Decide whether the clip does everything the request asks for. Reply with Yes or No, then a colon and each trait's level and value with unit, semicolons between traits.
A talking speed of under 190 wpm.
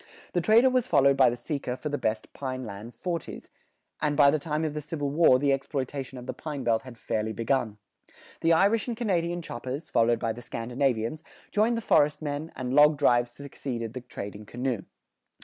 No: average, 195 wpm